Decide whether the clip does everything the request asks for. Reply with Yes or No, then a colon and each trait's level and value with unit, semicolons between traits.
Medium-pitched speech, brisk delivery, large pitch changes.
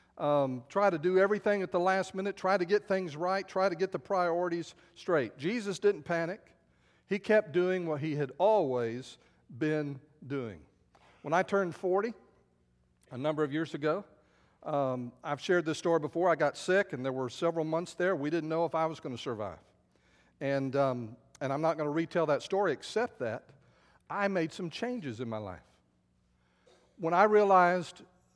No: medium, 160 Hz; average, 185 wpm; wide, 6.2 semitones